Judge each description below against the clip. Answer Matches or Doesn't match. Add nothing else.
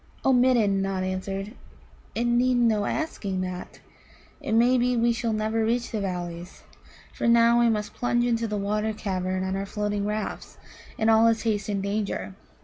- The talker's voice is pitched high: Matches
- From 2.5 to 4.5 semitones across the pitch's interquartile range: Matches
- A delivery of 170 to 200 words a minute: Matches